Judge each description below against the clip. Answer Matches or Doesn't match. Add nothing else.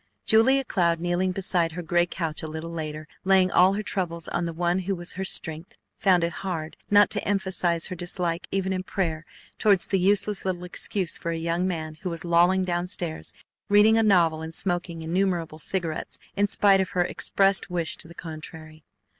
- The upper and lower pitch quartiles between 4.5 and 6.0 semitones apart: Doesn't match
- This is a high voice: Doesn't match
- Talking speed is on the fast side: Doesn't match